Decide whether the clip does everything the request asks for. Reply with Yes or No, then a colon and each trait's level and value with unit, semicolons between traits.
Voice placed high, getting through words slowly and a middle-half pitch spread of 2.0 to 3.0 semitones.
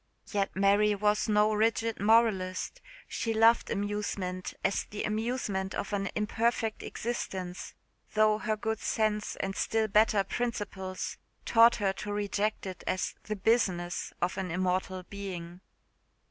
Yes: high, 210 Hz; slow, 130 wpm; narrow, 2.4 semitones